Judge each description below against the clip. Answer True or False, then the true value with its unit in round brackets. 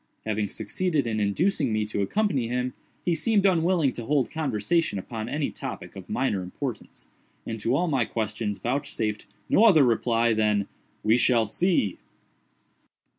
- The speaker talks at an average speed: True (150 wpm)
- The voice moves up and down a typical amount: False (6.2 semitones)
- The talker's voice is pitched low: True (120 Hz)